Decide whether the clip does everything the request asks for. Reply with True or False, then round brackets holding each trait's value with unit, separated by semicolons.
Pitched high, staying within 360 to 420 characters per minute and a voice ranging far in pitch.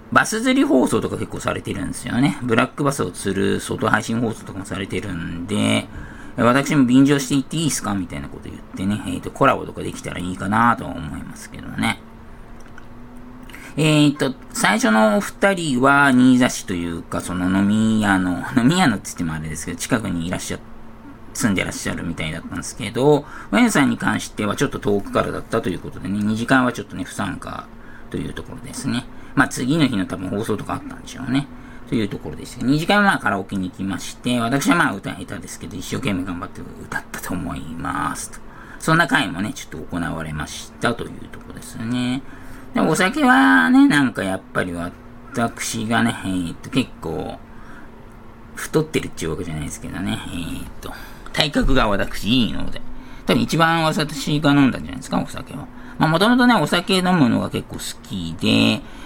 False (120 Hz; 400 characters per minute; 7.0 semitones)